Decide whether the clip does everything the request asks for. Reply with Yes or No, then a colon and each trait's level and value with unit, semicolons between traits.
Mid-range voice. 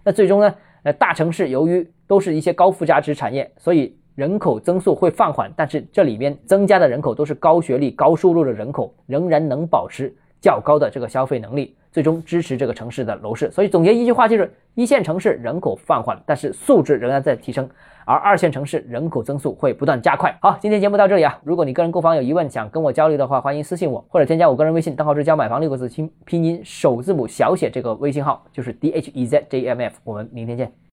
Yes: medium, 160 Hz